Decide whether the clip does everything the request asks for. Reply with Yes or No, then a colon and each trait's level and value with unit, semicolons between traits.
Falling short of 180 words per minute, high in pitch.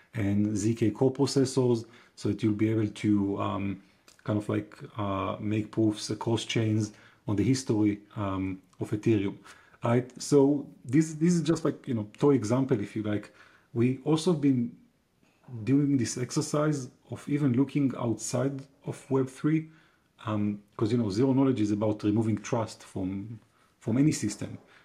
No: average, 160 wpm; low, 115 Hz